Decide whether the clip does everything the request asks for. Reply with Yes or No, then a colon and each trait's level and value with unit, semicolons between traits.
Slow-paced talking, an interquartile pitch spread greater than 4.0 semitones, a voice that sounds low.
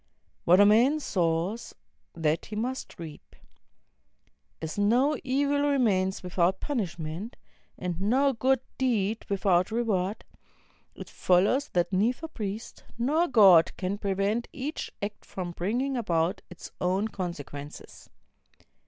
No: slow, 120 wpm; wide, 5.6 semitones; high, 205 Hz